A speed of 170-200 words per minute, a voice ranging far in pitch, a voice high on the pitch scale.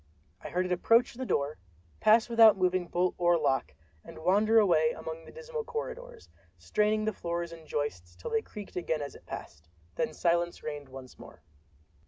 No: average, 175 wpm; wide, 7.2 semitones; medium, 175 Hz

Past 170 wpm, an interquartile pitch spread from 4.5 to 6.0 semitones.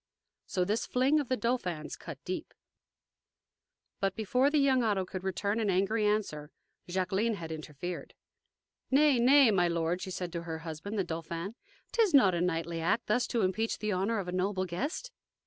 Yes: average, 180 wpm; average, 5.0 semitones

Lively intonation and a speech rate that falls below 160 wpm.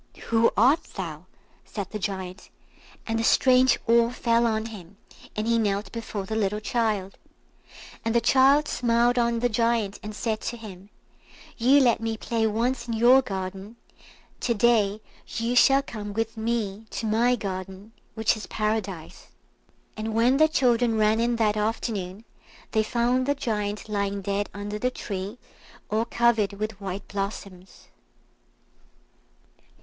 No: narrow, 2.6 semitones; average, 150 wpm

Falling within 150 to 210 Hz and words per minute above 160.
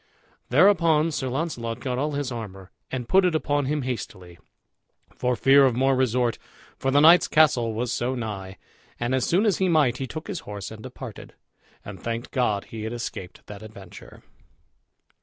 No: low, 125 Hz; average, 175 wpm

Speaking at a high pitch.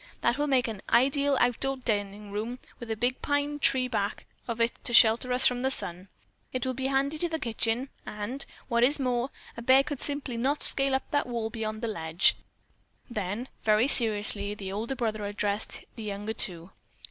Yes: high, 235 Hz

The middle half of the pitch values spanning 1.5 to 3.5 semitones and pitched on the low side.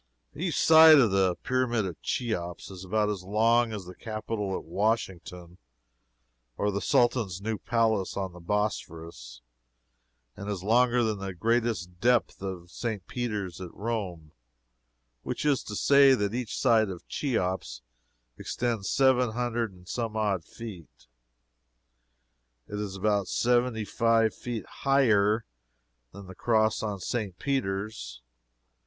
No: average, 3.9 semitones; low, 105 Hz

